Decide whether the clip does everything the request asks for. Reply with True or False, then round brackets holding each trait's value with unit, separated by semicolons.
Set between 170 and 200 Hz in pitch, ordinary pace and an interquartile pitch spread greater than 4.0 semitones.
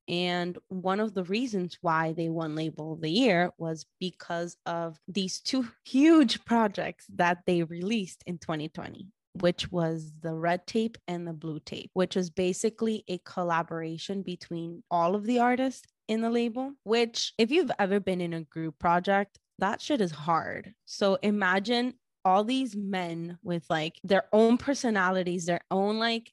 True (185 Hz; 165 wpm; 4.5 semitones)